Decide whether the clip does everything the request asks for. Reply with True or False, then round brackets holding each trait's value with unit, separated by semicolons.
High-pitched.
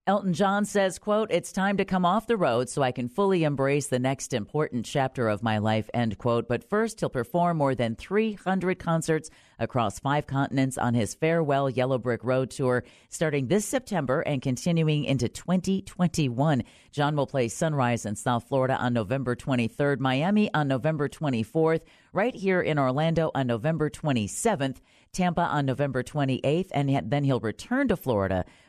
False (140 Hz)